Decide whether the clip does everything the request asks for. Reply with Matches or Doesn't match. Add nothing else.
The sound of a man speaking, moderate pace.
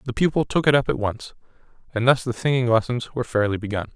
Doesn't match